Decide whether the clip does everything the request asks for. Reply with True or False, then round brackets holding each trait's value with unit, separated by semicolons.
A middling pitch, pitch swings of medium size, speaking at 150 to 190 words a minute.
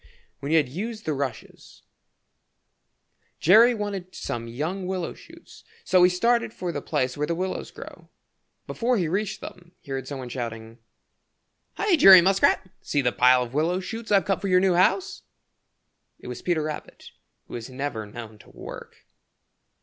False (175 Hz; 6.7 semitones; 170 wpm)